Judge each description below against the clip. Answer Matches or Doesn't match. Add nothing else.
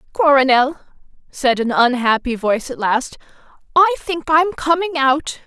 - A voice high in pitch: Matches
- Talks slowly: Matches